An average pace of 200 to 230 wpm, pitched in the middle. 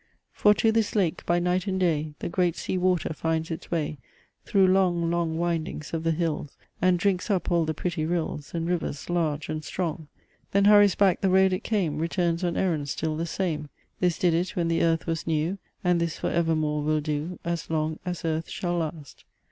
Yes: fast, 205 wpm; medium, 170 Hz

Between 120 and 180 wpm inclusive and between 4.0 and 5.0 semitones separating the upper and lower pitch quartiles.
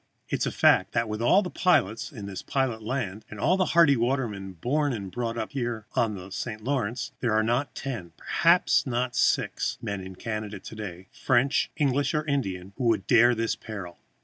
No: average, 200 wpm; average, 4.6 semitones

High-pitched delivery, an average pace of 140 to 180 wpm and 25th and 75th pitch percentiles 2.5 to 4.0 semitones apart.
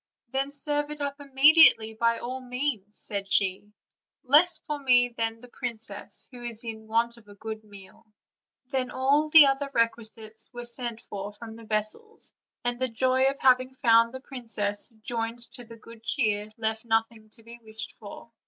Yes: high, 235 Hz; average, 170 wpm; average, 3.1 semitones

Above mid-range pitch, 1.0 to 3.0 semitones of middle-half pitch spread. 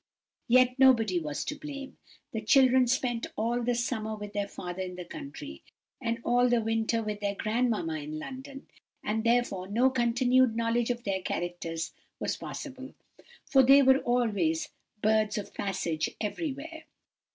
No: high, 230 Hz; average, 4.1 semitones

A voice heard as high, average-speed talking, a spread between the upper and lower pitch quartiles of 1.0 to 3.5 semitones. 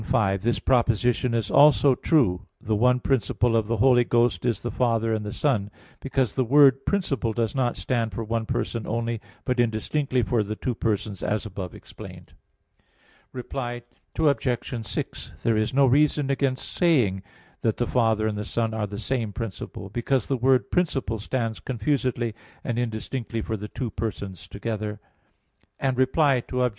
No: low, 120 Hz; average, 165 wpm; average, 3.1 semitones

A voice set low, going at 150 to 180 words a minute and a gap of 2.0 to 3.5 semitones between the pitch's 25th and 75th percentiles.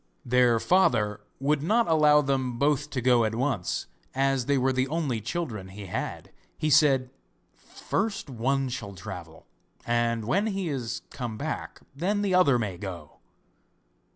No: low, 130 Hz; average, 155 wpm; average, 4.7 semitones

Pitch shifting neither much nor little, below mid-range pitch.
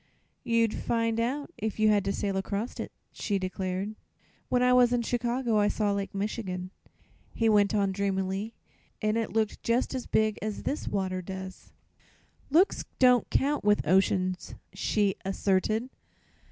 No: average, 3.2 semitones; high, 210 Hz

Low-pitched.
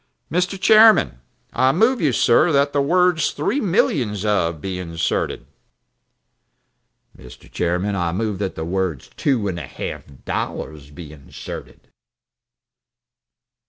Yes: low, 105 Hz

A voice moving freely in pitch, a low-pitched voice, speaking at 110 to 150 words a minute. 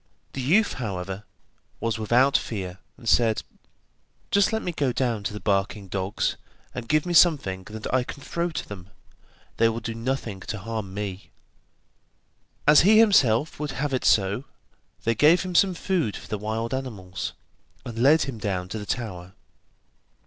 No: wide, 6.1 semitones; low, 115 Hz; average, 170 wpm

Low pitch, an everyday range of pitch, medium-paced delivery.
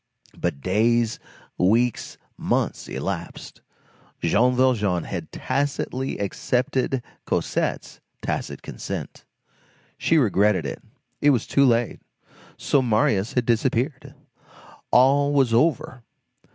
No: low, 120 Hz; average, 3.7 semitones; slow, 100 wpm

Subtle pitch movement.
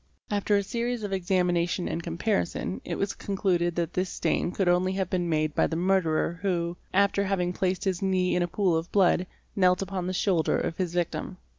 Yes: narrow, 1.9 semitones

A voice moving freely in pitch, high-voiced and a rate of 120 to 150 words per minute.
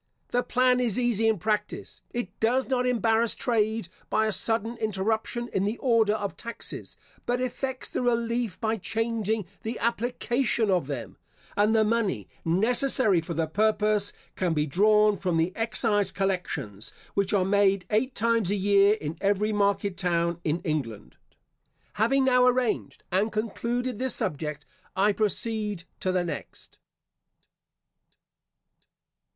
No: average, 3.7 semitones; high, 215 Hz; average, 140 wpm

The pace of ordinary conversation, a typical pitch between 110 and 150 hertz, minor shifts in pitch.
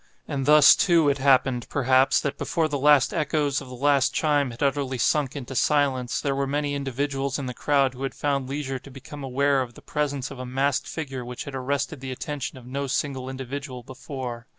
No: fast, 210 wpm; low, 135 Hz; narrow, 1.7 semitones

